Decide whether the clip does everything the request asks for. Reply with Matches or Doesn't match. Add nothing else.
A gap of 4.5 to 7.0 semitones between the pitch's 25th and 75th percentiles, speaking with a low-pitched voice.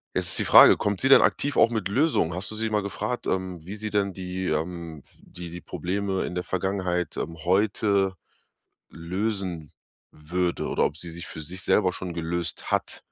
Doesn't match